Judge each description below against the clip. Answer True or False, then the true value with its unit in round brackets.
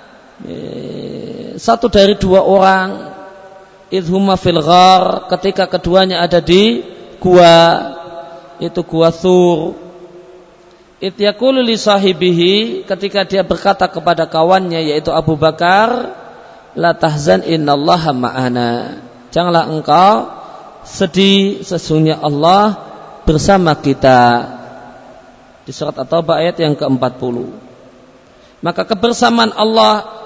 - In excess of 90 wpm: False (85 wpm)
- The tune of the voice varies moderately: True (3.2 semitones)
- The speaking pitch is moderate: True (175 Hz)